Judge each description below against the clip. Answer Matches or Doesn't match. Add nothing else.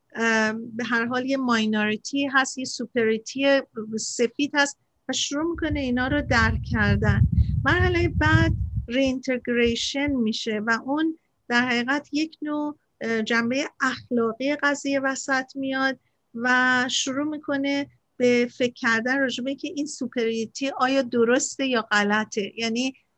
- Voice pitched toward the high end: Matches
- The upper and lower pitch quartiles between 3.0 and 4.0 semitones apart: Matches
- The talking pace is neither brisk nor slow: Matches